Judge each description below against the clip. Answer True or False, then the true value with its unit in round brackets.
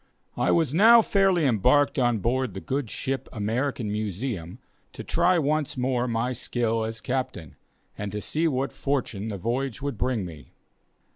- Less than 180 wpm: True (165 wpm)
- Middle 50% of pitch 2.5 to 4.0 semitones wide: False (4.6 semitones)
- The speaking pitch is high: False (125 Hz)